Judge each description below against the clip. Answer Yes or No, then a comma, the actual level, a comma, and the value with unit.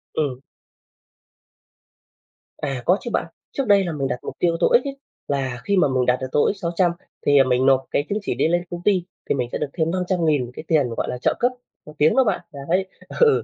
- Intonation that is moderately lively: No, wide, 5.8 semitones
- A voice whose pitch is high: No, medium, 160 Hz